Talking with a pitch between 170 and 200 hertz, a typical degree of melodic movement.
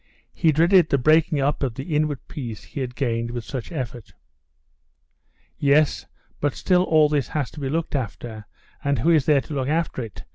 No: medium, 140 Hz; average, 3.8 semitones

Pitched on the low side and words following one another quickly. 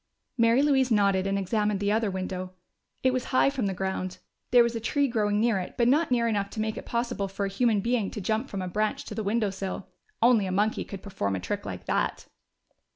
No: high, 210 Hz; fast, 235 wpm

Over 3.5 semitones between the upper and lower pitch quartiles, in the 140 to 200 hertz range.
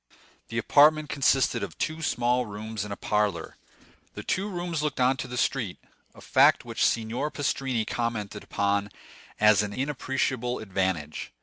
No: average, 4.9 semitones; low, 120 Hz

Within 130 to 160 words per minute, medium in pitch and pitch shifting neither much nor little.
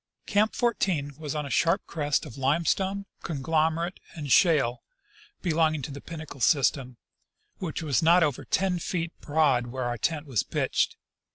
Yes: average, 155 wpm; medium, 155 Hz; average, 3.5 semitones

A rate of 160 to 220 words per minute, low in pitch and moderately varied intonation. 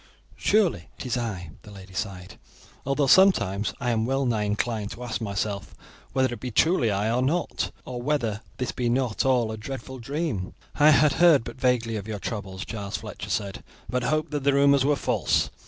Yes: average, 195 wpm; low, 120 Hz; average, 4.6 semitones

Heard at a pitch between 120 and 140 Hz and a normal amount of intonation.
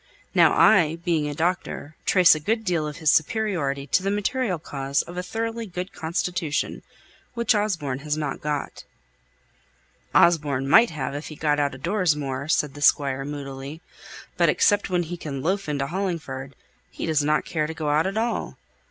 No: medium, 155 Hz; average, 4.1 semitones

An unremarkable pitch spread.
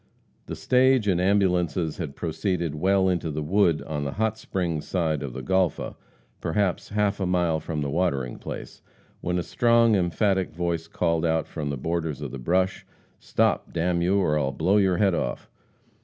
Yes: average, 3.4 semitones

